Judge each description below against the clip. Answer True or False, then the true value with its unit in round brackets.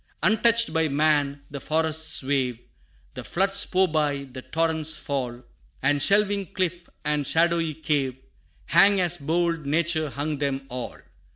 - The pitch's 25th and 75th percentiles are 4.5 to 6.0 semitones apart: False (3.2 semitones)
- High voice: False (155 Hz)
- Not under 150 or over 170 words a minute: False (135 wpm)